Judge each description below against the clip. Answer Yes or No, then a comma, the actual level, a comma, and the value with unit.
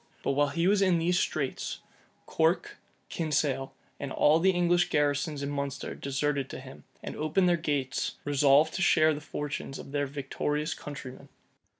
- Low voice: No, medium, 145 Hz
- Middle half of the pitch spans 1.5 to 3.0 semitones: Yes, average, 2.7 semitones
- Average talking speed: Yes, average, 165 wpm